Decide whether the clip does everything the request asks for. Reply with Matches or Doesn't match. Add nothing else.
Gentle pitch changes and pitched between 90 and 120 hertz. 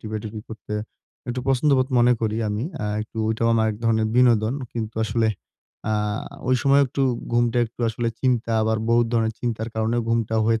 Matches